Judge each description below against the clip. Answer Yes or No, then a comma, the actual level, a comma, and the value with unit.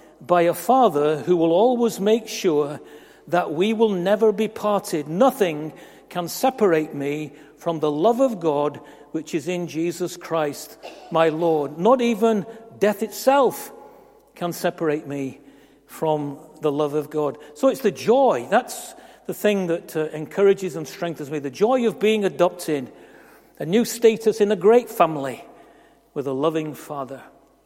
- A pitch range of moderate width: No, wide, 5.9 semitones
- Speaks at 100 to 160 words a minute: Yes, average, 155 wpm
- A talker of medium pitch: Yes, medium, 175 Hz